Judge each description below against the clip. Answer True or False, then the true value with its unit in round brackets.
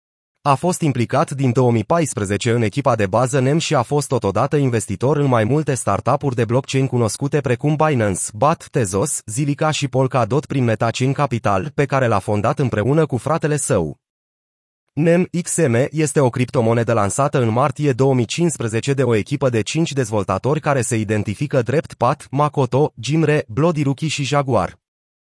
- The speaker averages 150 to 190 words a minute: True (155 wpm)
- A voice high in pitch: False (135 Hz)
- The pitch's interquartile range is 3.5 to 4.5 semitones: True (4.2 semitones)